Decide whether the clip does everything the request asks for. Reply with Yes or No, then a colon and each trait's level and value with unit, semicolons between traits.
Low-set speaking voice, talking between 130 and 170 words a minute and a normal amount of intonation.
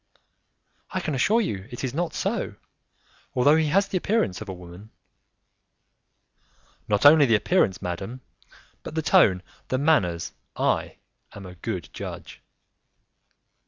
No: low, 130 Hz; slow, 135 wpm; wide, 8.9 semitones